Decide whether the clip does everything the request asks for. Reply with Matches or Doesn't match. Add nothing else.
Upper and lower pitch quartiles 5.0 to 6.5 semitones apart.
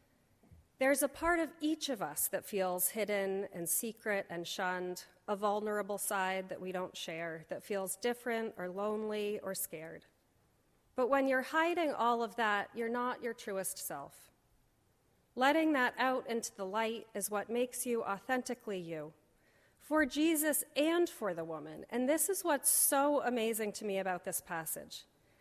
Matches